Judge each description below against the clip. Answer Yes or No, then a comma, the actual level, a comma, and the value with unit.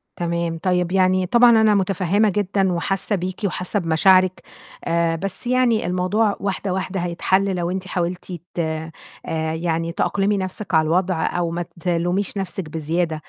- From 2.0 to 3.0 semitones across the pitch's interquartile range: Yes, narrow, 2.5 semitones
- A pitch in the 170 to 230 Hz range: Yes, medium, 185 Hz